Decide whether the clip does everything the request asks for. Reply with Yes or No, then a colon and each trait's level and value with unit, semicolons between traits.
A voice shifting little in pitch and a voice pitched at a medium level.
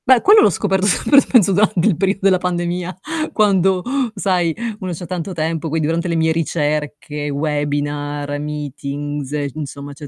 No: average, 4.1 semitones; medium, 165 Hz